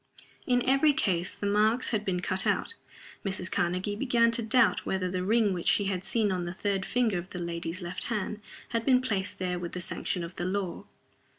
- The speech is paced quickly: Yes, fast, 210 wpm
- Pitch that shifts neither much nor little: Yes, average, 4.0 semitones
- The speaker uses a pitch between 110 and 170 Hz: No, high, 195 Hz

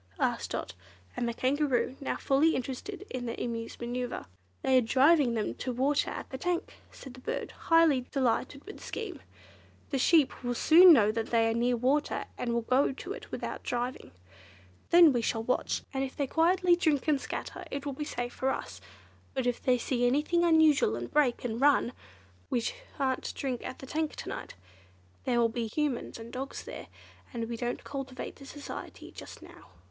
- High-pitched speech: Yes, very high, 260 Hz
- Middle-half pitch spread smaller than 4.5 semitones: Yes, average, 3.6 semitones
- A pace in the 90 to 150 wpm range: No, average, 195 wpm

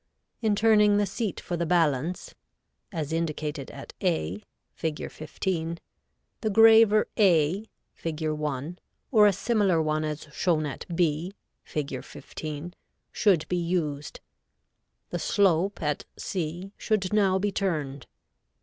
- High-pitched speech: No, medium, 170 Hz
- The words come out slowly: Yes, slow, 125 wpm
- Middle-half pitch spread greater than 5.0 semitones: No, average, 4.5 semitones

